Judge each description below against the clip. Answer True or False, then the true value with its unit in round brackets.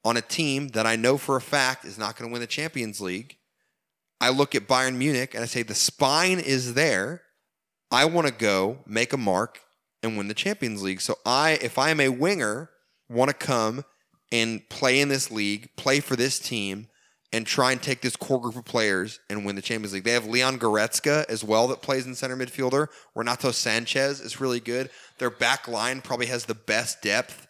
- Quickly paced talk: True (215 wpm)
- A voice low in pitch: True (125 Hz)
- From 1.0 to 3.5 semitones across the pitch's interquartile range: True (3.2 semitones)